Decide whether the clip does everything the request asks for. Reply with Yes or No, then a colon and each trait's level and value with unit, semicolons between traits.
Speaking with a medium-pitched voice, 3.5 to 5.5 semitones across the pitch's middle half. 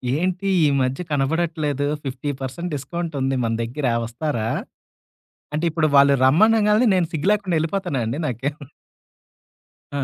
Yes: medium, 150 Hz; average, 4.6 semitones